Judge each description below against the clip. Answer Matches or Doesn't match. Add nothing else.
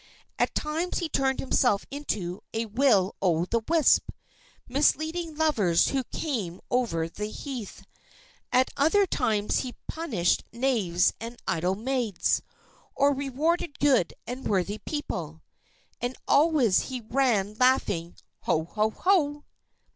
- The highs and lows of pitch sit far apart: Matches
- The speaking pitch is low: Doesn't match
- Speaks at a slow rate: Matches